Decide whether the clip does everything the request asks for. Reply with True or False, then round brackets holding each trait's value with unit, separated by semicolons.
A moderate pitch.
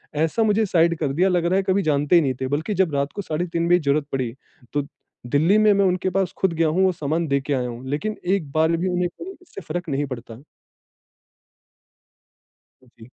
True (165 Hz)